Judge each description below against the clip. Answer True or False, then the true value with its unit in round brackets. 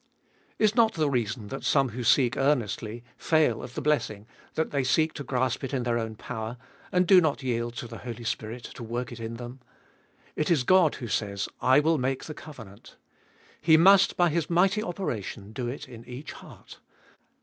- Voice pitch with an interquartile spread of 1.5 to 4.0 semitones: False (5.1 semitones)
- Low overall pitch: True (130 Hz)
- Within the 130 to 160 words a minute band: False (200 wpm)